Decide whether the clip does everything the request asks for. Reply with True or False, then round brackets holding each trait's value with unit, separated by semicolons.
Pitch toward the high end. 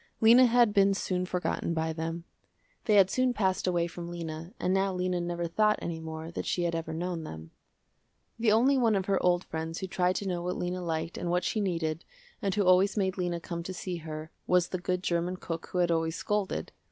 False (180 Hz)